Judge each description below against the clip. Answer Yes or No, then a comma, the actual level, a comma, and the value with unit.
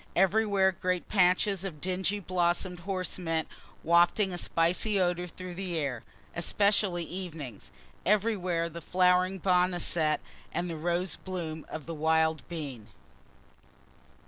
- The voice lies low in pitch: No, medium, 180 Hz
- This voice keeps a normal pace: No, slow, 120 wpm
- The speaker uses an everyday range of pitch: No, narrow, 2.3 semitones